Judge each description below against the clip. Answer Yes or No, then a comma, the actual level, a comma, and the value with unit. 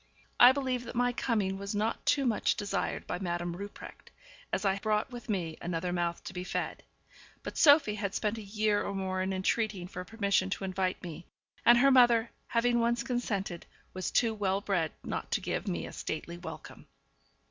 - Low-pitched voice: No, high, 200 Hz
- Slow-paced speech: No, average, 190 wpm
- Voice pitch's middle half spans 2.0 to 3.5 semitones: No, average, 4.1 semitones